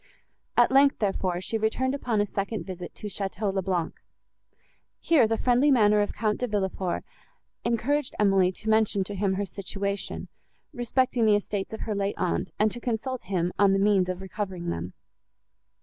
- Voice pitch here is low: No, high, 205 Hz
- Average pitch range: Yes, average, 3.0 semitones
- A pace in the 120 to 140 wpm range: No, average, 175 wpm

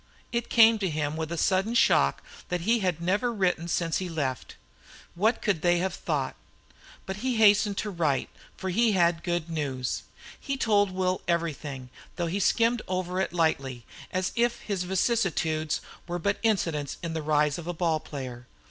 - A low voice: No, medium, 175 Hz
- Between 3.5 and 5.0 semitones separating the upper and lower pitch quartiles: Yes, average, 4.3 semitones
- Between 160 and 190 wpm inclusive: Yes, average, 175 wpm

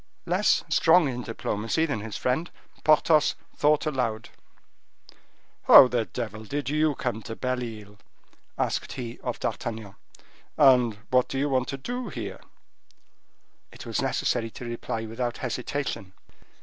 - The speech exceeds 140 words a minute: No, slow, 135 wpm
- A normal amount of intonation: Yes, average, 4.1 semitones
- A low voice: Yes, low, 125 Hz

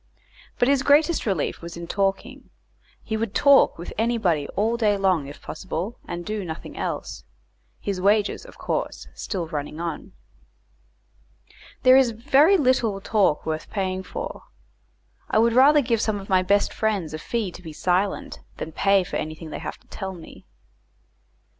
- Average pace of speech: Yes, average, 165 wpm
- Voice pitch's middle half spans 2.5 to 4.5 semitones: No, average, 5.1 semitones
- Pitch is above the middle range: Yes, high, 200 Hz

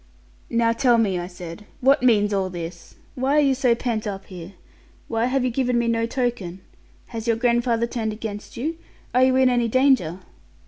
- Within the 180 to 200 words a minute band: Yes, average, 190 wpm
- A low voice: No, high, 230 Hz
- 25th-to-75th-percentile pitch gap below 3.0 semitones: No, average, 3.6 semitones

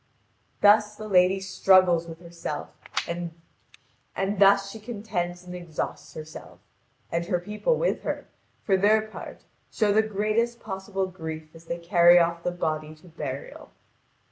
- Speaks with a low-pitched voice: No, medium, 180 Hz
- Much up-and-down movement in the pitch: No, average, 3.4 semitones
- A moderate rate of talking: Yes, average, 145 wpm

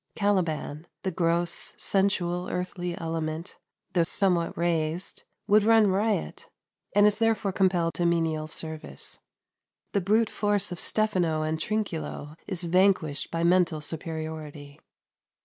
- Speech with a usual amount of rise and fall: Yes, average, 3.6 semitones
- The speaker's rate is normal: No, slow, 120 wpm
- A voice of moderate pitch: Yes, medium, 175 Hz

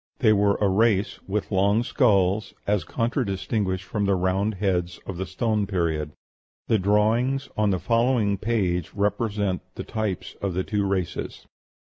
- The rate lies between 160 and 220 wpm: No, average, 150 wpm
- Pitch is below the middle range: Yes, low, 100 Hz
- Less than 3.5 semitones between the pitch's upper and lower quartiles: Yes, narrow, 2.6 semitones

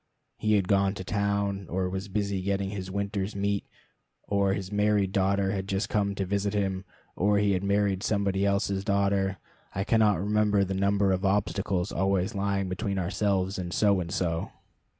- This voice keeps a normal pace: Yes, average, 175 wpm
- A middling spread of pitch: No, narrow, 1.0 semitones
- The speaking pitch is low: Yes, low, 100 Hz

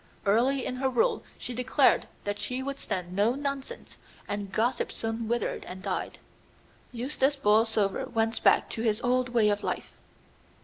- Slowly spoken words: No, average, 160 wpm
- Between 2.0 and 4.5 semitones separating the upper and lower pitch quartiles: Yes, average, 3.6 semitones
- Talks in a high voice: Yes, high, 235 Hz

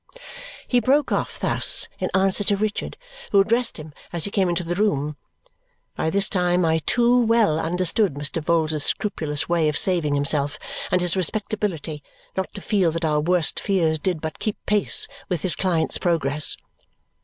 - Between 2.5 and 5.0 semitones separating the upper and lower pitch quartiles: Yes, average, 4.2 semitones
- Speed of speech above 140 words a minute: Yes, average, 170 wpm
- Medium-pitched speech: Yes, medium, 175 Hz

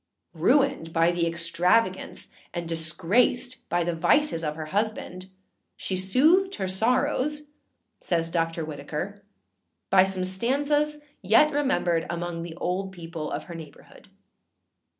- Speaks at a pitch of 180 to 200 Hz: Yes, medium, 185 Hz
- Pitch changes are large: Yes, wide, 6.7 semitones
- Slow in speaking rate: Yes, slow, 125 wpm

